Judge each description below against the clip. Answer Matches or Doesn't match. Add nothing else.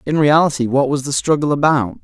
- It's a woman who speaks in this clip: Doesn't match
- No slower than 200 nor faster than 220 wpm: Matches